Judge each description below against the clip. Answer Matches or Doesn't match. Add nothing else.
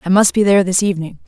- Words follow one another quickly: Matches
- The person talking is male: Doesn't match